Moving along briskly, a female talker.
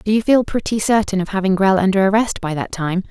Yes: fast, 250 wpm; female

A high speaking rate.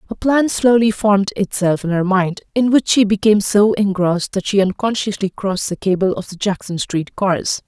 No: average, 195 wpm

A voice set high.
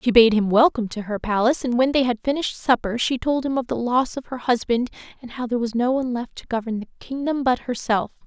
Yes: high, 245 Hz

